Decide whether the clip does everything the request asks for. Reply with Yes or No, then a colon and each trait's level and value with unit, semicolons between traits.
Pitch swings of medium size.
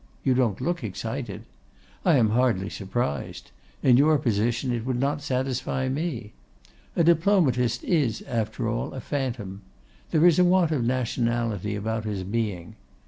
Yes: average, 4.3 semitones